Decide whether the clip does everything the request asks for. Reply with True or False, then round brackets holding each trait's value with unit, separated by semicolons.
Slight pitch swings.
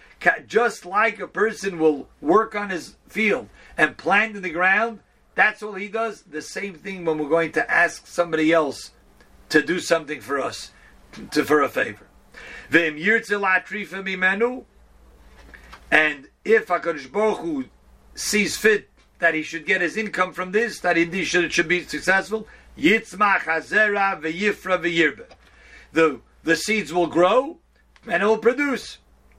False (4.8 semitones)